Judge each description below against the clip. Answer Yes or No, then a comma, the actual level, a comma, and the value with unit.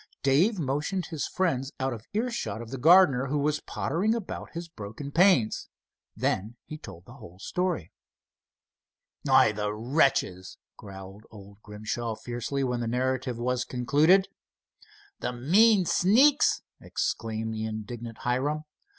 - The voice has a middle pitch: No, low, 130 Hz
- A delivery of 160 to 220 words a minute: No, slow, 135 wpm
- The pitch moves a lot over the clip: Yes, wide, 6.6 semitones